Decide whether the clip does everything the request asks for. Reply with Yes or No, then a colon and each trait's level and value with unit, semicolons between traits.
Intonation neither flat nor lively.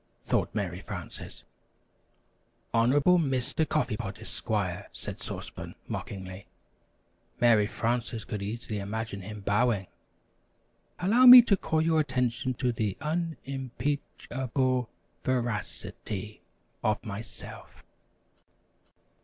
Yes: average, 4.7 semitones